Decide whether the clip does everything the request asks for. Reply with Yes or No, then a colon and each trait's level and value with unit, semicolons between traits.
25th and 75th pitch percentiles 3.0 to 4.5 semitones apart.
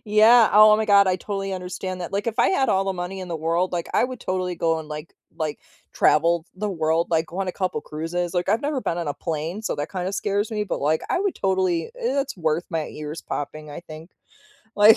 Yes: average, 4.0 semitones